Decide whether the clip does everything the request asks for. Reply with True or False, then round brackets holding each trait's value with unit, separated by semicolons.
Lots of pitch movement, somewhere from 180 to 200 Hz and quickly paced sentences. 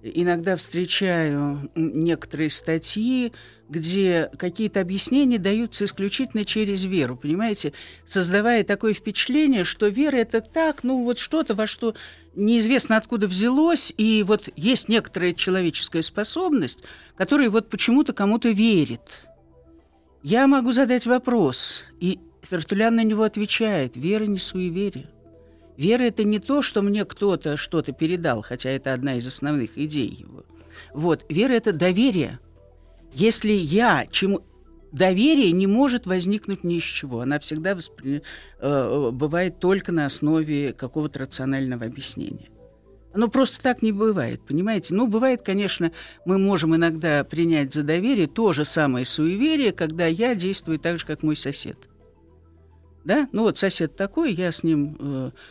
False (6.5 semitones; 185 Hz; 135 wpm)